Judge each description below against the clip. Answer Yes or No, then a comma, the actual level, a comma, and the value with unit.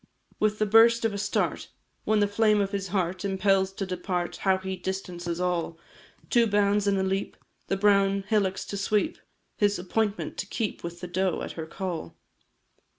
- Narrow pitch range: Yes, narrow, 1.9 semitones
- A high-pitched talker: Yes, high, 195 Hz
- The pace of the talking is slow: No, average, 180 wpm